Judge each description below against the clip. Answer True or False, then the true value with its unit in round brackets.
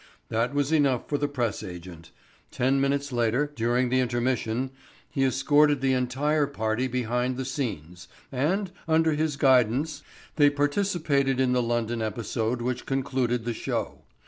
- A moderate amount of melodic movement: True (3.2 semitones)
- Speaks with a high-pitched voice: False (130 Hz)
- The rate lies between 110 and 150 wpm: True (145 wpm)